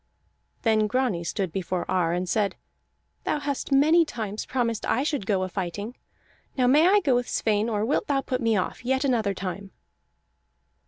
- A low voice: No, high, 225 Hz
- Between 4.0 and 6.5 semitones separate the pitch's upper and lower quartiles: Yes, average, 5.2 semitones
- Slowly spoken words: No, average, 175 wpm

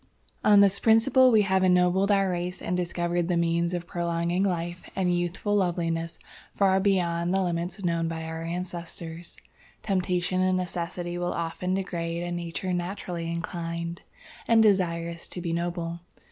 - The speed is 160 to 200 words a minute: No, average, 150 wpm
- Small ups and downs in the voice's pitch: Yes, narrow, 1.8 semitones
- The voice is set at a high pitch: No, medium, 175 Hz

